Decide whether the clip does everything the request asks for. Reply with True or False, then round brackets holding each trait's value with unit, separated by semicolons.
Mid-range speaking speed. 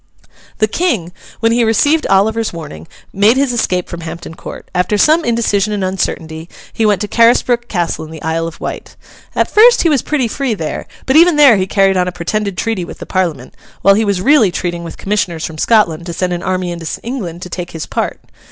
False (215 wpm)